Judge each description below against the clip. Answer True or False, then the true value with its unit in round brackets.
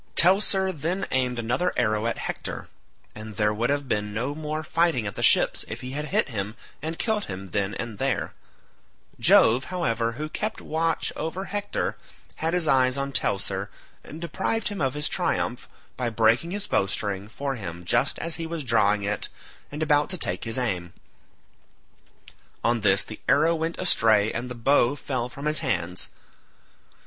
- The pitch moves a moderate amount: False (6.9 semitones)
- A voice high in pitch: False (130 Hz)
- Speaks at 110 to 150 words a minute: False (175 wpm)